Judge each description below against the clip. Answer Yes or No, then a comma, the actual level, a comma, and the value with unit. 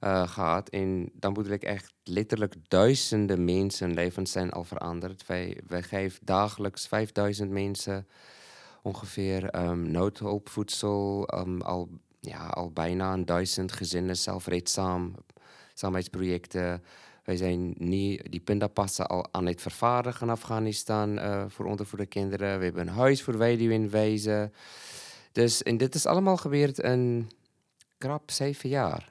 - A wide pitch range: No, average, 3.0 semitones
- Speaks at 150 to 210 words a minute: No, average, 140 wpm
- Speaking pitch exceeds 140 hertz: No, low, 100 Hz